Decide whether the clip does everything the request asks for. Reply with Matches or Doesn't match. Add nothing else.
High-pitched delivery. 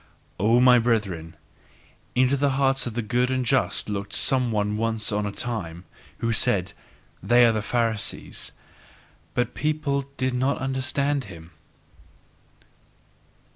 Doesn't match